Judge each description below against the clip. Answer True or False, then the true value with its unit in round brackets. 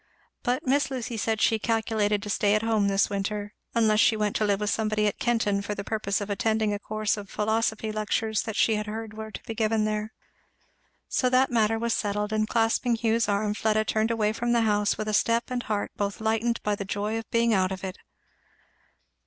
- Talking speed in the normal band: False (215 wpm)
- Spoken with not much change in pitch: True (1.4 semitones)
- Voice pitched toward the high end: True (215 Hz)